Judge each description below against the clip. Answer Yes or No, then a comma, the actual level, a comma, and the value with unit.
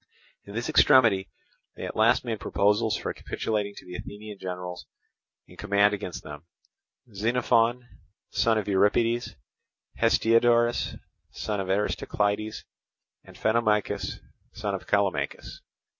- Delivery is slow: Yes, slow, 115 wpm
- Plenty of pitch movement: No, average, 2.7 semitones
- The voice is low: Yes, low, 105 Hz